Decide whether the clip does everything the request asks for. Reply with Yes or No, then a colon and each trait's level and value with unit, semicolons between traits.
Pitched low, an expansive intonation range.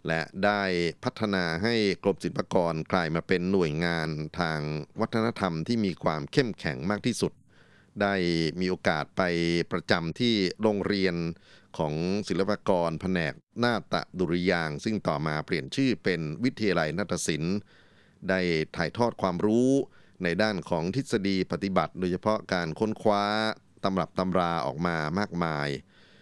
No: very low, 95 Hz; average, 4.1 semitones